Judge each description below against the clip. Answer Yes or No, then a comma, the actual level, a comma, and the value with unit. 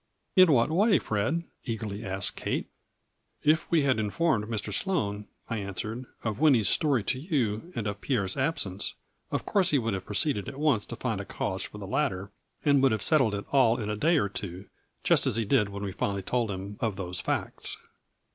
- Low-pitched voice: Yes, low, 110 Hz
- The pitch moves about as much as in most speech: No, wide, 5.8 semitones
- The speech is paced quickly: Yes, fast, 215 wpm